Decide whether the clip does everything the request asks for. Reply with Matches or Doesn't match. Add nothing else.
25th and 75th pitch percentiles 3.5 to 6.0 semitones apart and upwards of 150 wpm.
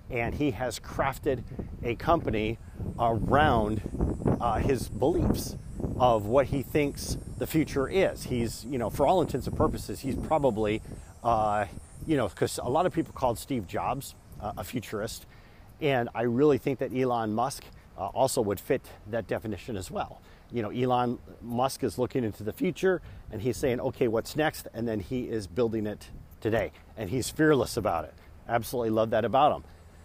Matches